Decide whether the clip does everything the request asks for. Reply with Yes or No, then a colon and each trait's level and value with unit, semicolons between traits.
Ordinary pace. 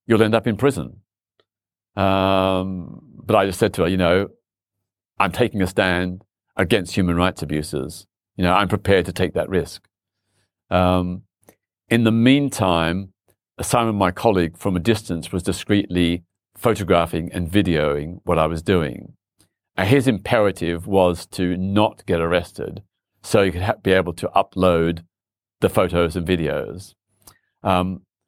Yes: average, 150 wpm